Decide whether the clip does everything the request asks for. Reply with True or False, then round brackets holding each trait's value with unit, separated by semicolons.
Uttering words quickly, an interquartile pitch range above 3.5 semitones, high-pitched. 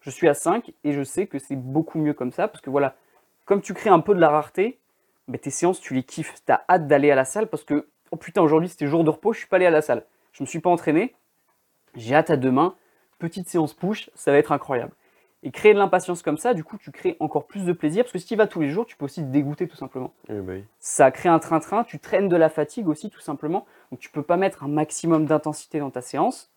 False (280 wpm; 3.9 semitones; 155 Hz)